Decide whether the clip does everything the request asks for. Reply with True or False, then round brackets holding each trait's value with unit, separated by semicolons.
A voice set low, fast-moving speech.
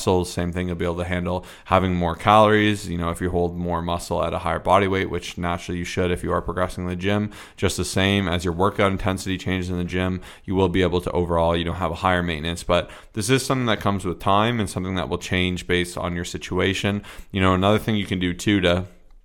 True (90 Hz; 260 wpm)